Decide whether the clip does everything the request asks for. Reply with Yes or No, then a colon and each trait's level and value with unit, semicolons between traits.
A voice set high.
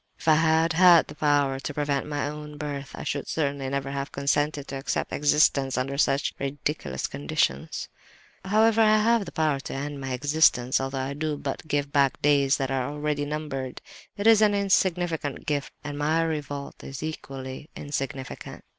No: medium, 145 Hz